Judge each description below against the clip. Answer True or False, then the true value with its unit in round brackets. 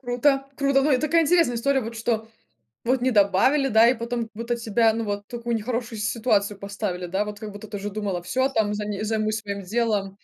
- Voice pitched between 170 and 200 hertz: False (225 Hz)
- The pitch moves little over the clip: False (3.0 semitones)